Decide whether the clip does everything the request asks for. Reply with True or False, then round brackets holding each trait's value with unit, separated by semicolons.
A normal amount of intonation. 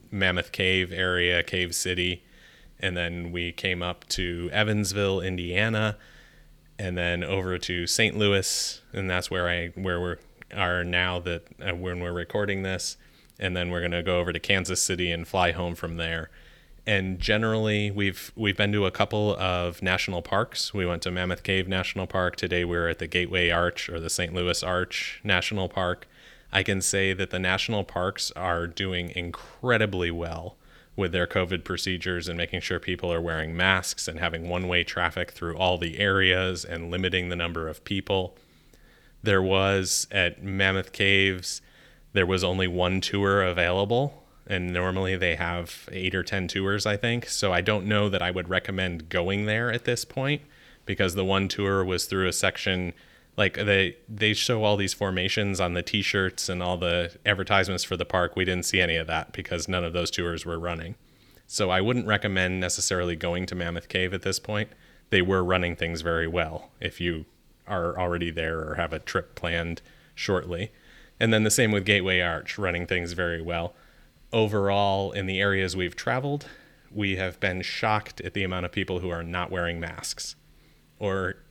False (2.0 semitones)